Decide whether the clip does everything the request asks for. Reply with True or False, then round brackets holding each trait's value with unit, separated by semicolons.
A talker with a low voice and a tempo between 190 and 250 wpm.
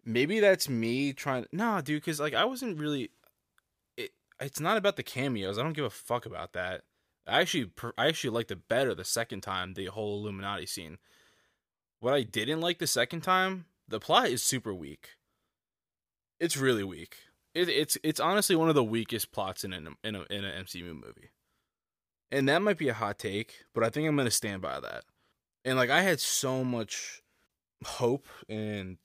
True (130 Hz; 195 wpm)